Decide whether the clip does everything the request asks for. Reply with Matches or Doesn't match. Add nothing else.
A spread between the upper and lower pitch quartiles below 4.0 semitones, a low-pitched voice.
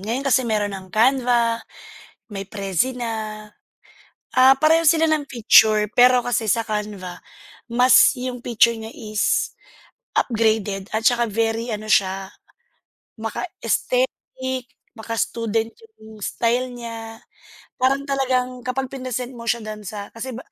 Doesn't match